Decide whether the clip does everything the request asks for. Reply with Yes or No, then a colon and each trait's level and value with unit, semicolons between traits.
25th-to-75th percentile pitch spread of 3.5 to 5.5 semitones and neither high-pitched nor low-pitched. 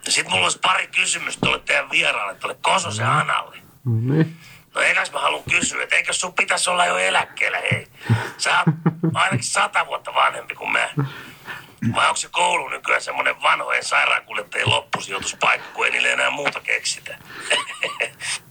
Yes: average, 3.9 semitones; medium, 160 Hz